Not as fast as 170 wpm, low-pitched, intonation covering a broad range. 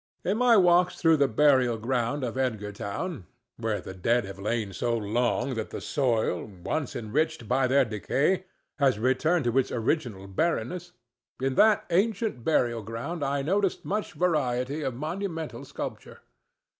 Yes: average, 145 wpm; low, 130 Hz; wide, 6.1 semitones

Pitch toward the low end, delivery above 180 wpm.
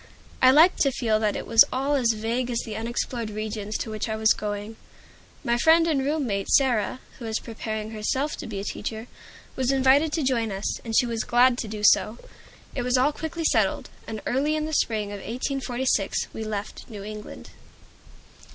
No: high, 230 Hz; average, 195 wpm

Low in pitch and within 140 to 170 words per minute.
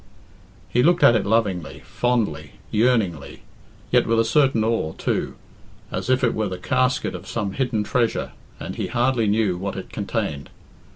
Yes: low, 110 Hz; average, 165 wpm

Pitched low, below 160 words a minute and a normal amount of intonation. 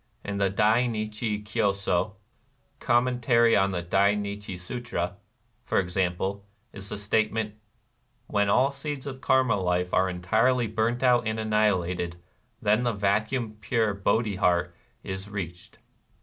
Yes: low, 105 Hz; average, 150 wpm; average, 3.3 semitones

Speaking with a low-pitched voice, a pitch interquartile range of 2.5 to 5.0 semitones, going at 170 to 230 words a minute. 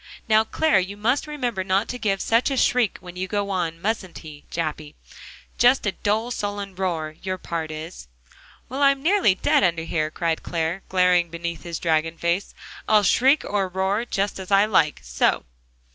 No: high, 190 Hz; average, 4.3 semitones; average, 180 wpm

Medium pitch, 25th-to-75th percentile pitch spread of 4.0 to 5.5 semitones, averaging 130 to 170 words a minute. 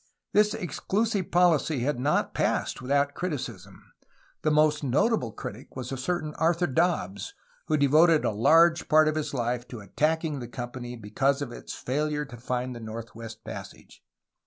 Yes: medium, 145 Hz; average, 4.7 semitones; average, 160 wpm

